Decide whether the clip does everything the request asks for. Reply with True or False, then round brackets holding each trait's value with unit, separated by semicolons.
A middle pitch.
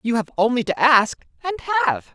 False (215 Hz)